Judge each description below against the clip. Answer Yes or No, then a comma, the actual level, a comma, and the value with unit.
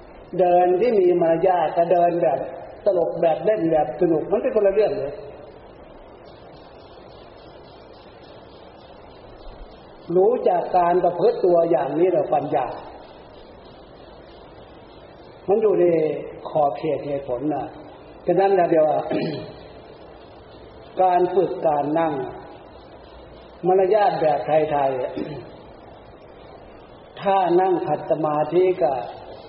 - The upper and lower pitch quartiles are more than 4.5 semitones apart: No, average, 4.1 semitones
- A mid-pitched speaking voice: Yes, medium, 175 Hz